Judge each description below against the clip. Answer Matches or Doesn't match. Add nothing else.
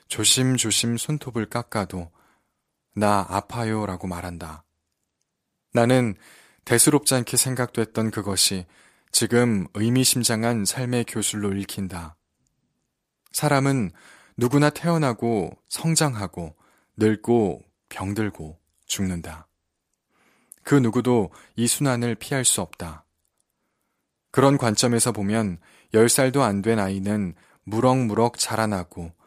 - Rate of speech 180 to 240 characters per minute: Matches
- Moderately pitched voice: Doesn't match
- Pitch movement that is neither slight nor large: Matches